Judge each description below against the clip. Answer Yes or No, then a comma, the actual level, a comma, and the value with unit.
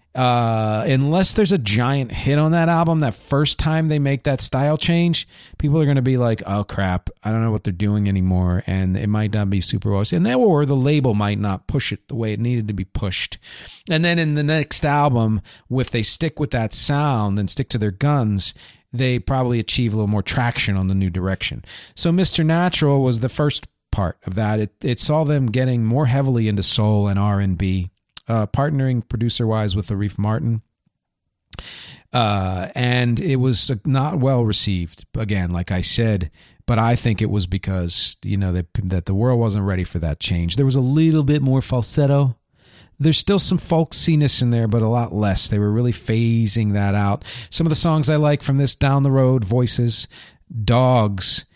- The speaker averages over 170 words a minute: Yes, fast, 205 wpm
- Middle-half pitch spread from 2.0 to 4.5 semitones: No, average, 5.2 semitones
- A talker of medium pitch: No, low, 120 Hz